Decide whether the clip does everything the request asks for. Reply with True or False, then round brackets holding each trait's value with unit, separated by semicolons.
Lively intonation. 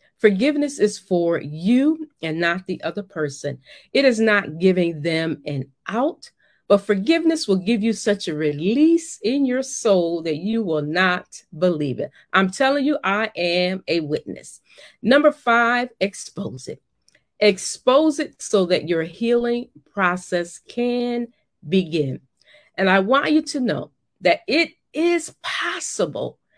True (6.7 semitones)